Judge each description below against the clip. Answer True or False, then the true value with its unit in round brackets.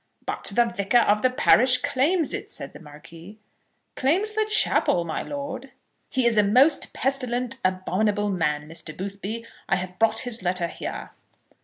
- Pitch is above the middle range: True (215 Hz)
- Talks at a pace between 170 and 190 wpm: False (160 wpm)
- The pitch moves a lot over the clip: True (5.8 semitones)